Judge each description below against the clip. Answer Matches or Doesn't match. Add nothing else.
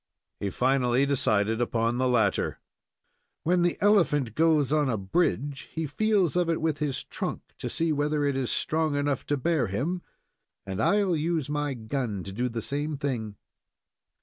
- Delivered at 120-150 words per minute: Doesn't match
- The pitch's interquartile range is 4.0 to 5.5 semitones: Matches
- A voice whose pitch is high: Doesn't match